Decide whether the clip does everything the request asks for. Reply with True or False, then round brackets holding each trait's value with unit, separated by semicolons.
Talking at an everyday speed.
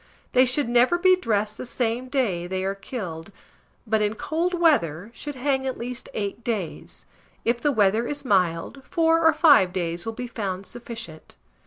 True (175 wpm)